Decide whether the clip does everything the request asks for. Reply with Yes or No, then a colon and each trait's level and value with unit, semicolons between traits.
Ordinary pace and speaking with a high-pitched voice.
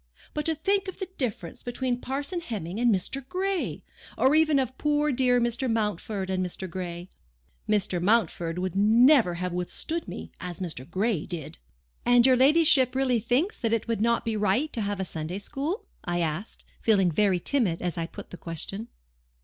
Yes: average, 180 wpm; high, 225 Hz